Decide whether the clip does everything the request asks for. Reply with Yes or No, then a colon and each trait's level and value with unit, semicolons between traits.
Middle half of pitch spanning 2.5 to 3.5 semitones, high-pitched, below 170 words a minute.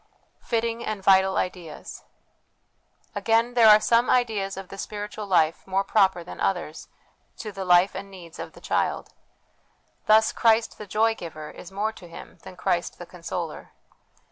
Yes: average, 3.2 semitones; high, 195 Hz; average, 160 wpm